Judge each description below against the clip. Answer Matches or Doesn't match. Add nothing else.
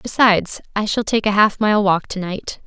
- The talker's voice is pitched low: Doesn't match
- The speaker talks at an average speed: Doesn't match